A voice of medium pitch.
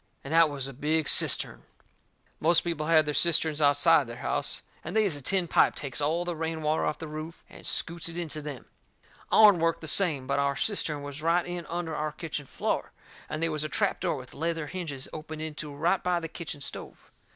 Yes: medium, 155 Hz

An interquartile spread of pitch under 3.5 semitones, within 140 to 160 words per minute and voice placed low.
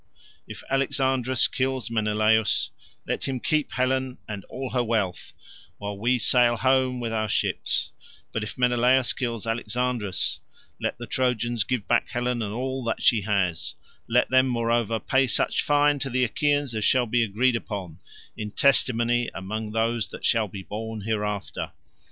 Yes: average, 3.0 semitones; average, 155 wpm; low, 120 Hz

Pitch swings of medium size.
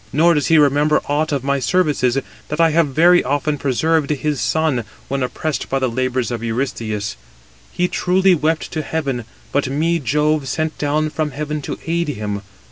Yes: average, 3.2 semitones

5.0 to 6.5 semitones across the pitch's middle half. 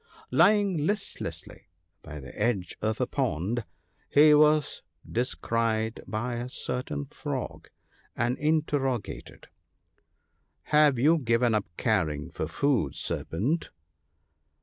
Yes: average, 5.3 semitones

